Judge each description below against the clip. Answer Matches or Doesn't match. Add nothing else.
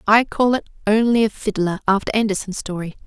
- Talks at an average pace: Matches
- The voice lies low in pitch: Doesn't match